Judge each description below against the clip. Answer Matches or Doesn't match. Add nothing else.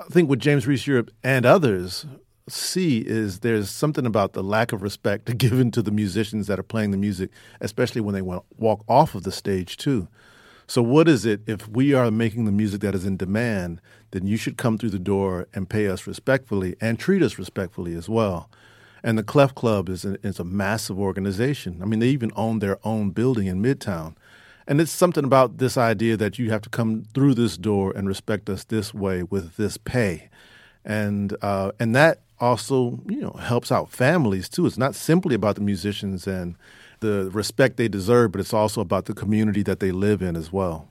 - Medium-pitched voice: Doesn't match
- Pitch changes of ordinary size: Matches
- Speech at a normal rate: Doesn't match